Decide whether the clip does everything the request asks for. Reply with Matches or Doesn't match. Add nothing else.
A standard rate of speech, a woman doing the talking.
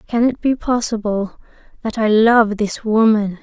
Matches